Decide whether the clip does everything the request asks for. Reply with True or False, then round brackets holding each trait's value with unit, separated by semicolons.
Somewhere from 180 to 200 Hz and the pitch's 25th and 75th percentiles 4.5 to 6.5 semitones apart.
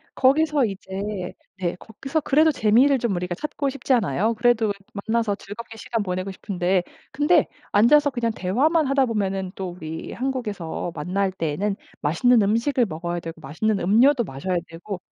False (210 Hz; 5.5 semitones)